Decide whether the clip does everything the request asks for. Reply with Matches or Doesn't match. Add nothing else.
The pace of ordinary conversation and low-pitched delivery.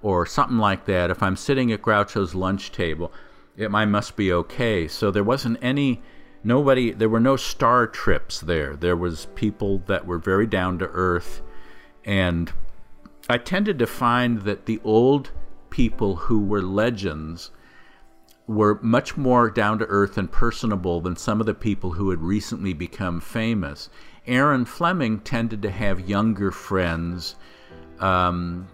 Matches